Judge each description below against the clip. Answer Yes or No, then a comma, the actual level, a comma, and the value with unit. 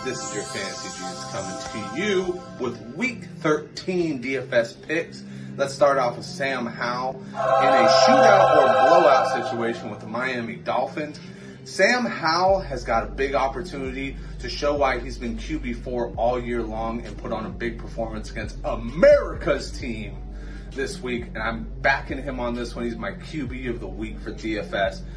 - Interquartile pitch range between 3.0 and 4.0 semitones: No, average, 4.7 semitones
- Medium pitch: No, low, 125 Hz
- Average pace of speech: Yes, average, 170 wpm